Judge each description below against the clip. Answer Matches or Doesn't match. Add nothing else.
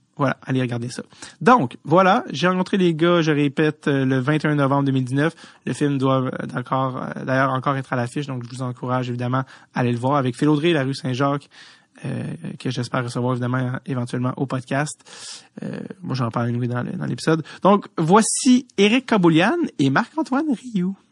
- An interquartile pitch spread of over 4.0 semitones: Matches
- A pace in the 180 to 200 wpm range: Doesn't match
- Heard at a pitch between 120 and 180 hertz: Matches